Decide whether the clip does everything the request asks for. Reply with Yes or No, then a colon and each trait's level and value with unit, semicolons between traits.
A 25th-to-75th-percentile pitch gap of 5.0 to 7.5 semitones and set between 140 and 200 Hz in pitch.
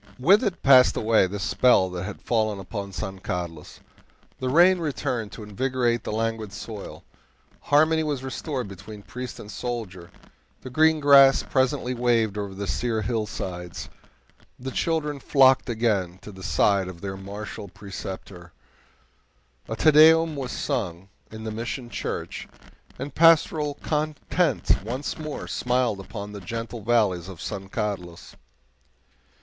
No: average, 5.3 semitones; low, 115 Hz